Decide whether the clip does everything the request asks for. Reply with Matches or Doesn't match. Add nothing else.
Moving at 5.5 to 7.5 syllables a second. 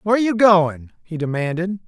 Matches